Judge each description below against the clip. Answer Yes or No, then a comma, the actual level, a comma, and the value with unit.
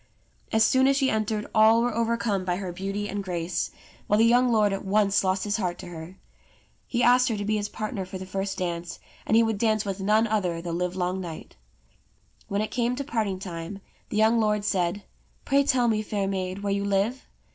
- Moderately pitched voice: No, high, 205 Hz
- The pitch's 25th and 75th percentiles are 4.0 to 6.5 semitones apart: No, average, 3.0 semitones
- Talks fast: Yes, fast, 220 wpm